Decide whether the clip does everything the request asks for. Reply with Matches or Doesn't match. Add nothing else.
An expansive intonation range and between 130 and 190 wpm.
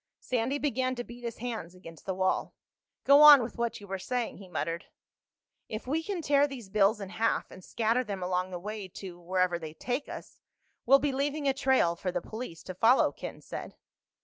Doesn't match